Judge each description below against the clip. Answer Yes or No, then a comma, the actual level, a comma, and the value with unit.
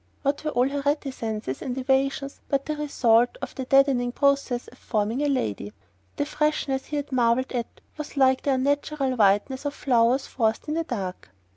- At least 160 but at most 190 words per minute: Yes, average, 180 wpm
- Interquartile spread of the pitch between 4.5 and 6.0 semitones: No, average, 2.9 semitones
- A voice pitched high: Yes, very high, 265 Hz